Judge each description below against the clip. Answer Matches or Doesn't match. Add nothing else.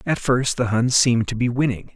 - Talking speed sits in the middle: Doesn't match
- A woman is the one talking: Doesn't match